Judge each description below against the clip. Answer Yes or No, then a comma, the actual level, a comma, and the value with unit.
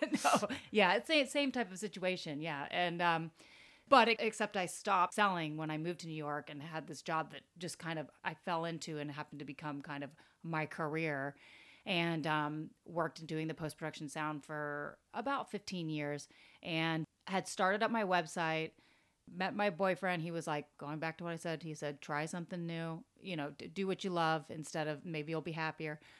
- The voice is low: No, medium, 160 Hz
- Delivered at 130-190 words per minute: No, fast, 205 wpm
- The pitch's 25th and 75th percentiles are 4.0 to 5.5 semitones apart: No, average, 3.2 semitones